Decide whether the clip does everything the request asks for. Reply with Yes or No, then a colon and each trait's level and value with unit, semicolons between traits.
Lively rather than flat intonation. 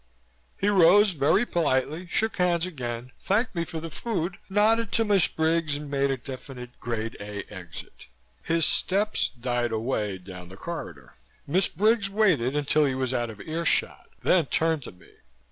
Yes: wide, 7.2 semitones